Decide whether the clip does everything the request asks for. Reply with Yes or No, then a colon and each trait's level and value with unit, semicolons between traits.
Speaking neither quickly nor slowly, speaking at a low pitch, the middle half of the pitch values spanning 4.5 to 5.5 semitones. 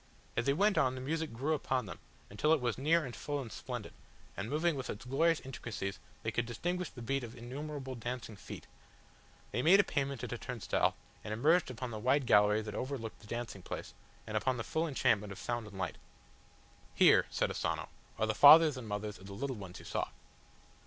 No: fast, 210 wpm; low, 125 Hz; average, 4.9 semitones